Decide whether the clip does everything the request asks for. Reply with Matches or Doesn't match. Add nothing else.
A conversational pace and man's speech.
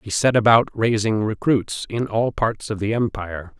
Matches